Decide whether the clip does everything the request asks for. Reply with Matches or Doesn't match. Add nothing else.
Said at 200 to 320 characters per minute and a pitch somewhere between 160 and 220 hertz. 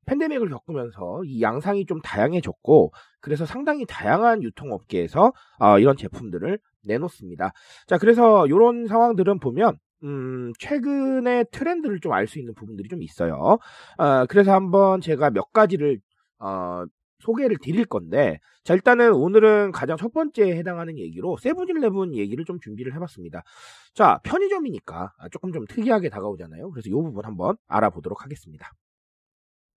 Doesn't match